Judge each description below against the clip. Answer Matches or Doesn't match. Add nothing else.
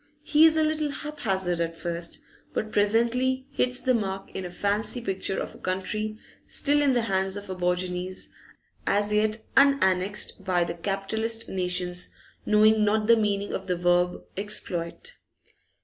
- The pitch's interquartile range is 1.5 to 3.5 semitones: Doesn't match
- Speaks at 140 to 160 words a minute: Matches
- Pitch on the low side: Doesn't match